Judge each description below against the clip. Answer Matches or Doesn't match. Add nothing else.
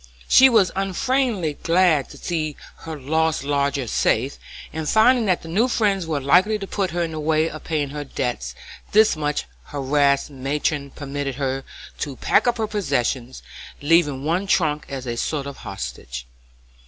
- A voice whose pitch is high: Doesn't match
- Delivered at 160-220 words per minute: Matches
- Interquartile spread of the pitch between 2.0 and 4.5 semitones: Doesn't match